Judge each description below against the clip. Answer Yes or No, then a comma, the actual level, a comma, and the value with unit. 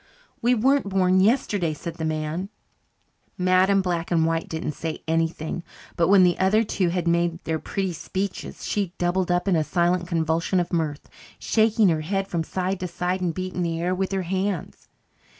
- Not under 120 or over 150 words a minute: No, average, 185 wpm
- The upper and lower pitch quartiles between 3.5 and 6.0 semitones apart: No, narrow, 2.5 semitones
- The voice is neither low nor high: Yes, medium, 180 Hz